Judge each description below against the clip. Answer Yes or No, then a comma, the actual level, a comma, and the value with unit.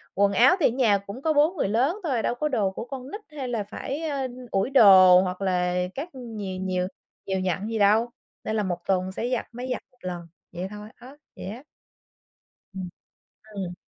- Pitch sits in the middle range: No, high, 215 Hz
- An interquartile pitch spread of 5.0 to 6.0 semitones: Yes, average, 5.3 semitones